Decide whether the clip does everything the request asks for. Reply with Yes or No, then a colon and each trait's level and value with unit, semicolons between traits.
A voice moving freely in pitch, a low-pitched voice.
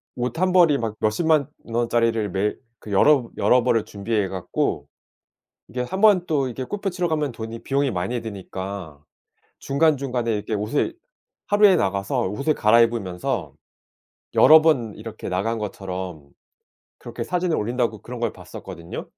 Yes: wide, 6.0 semitones; low, 115 Hz